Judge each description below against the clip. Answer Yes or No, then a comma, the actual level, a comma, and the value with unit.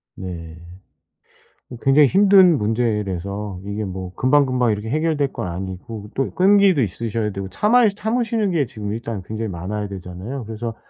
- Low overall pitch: Yes, low, 110 Hz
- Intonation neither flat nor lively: No, wide, 6.9 semitones